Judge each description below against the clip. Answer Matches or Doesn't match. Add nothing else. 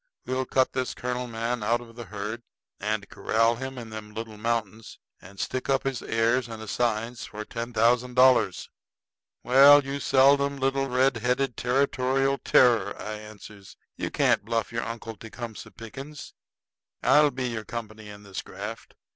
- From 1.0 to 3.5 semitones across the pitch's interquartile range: Matches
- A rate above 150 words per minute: Matches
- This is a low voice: Matches